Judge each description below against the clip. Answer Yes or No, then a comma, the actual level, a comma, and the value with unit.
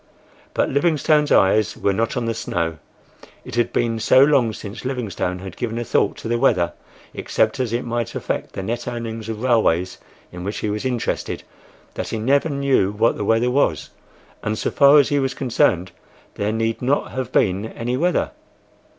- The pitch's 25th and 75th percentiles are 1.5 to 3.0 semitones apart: No, average, 3.5 semitones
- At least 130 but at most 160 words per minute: No, average, 185 wpm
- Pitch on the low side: Yes, low, 115 Hz